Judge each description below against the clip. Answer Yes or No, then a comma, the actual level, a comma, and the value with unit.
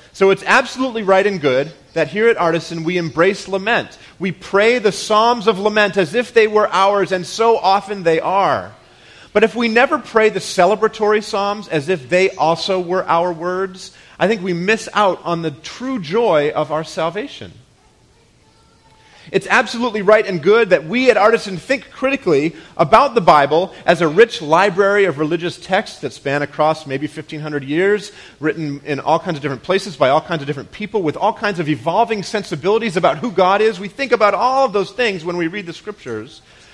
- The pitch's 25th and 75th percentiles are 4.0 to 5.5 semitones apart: Yes, average, 4.7 semitones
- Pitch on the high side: Yes, high, 195 Hz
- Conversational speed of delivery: Yes, average, 195 wpm